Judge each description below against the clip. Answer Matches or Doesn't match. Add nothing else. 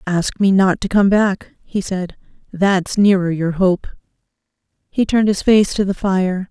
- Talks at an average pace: Matches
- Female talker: Matches